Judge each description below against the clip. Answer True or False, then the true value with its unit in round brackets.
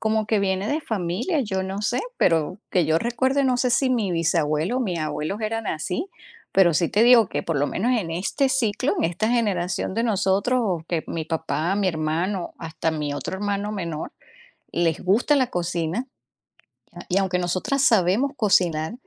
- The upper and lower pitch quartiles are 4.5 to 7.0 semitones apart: True (5.2 semitones)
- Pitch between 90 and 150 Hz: False (190 Hz)